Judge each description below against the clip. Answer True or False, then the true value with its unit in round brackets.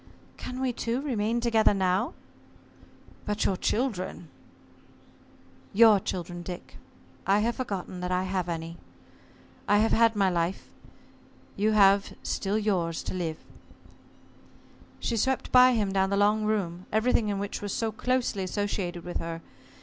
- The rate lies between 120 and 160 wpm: True (140 wpm)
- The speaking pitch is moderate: False (205 Hz)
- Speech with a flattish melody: False (3.4 semitones)